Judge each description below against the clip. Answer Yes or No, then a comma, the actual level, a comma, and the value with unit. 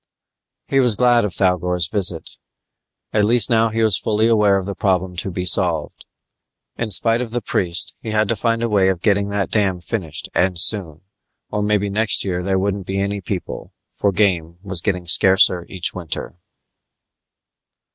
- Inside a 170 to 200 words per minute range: Yes, average, 175 wpm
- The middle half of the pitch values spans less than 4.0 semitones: Yes, average, 2.9 semitones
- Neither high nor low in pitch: No, low, 100 Hz